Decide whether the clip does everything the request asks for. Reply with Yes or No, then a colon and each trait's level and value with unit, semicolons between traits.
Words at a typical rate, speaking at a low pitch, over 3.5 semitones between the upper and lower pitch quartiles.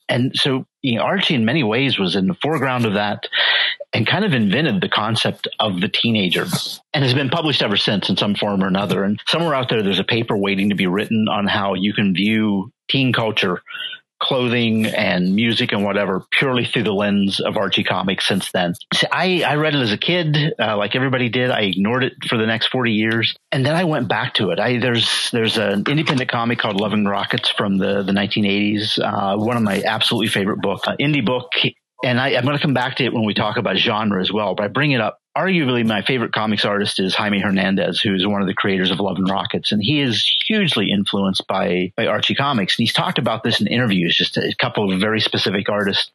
No: fast, 230 wpm; low, 110 Hz; average, 3.9 semitones